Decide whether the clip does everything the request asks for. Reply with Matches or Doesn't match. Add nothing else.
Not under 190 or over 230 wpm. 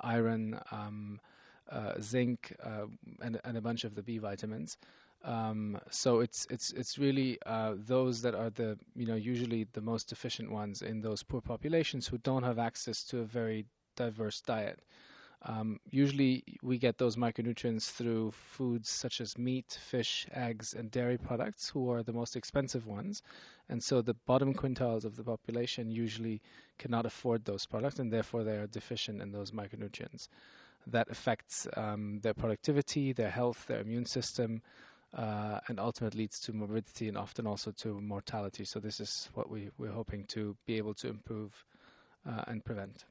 Doesn't match